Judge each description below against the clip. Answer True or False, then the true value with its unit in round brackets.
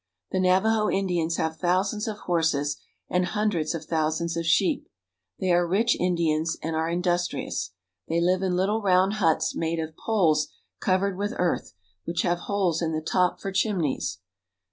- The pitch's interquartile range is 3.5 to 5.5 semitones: False (2.9 semitones)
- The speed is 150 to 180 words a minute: True (165 wpm)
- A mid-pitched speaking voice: True (175 Hz)